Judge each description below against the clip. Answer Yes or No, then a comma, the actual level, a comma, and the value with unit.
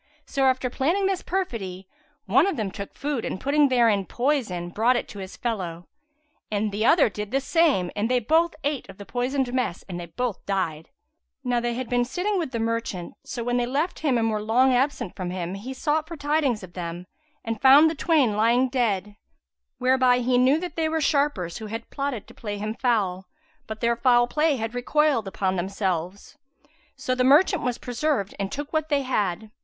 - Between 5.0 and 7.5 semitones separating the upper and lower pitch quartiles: Yes, wide, 5.4 semitones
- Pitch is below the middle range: No, high, 245 Hz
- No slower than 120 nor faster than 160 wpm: No, average, 200 wpm